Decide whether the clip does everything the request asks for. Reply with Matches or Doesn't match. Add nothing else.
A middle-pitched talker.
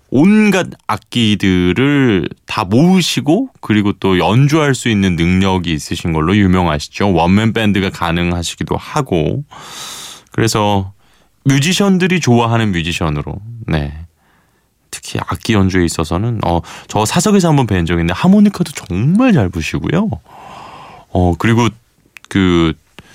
Doesn't match